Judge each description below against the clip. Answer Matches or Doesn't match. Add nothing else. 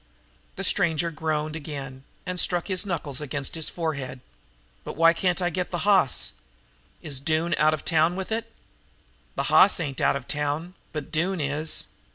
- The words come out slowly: Doesn't match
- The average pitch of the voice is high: Doesn't match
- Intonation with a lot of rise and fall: Doesn't match